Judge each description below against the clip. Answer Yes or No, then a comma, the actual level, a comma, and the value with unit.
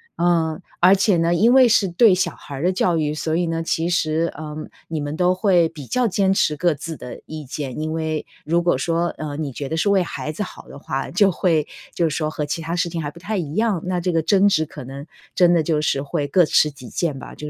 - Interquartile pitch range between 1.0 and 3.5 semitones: Yes, average, 2.9 semitones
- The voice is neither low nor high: Yes, medium, 165 Hz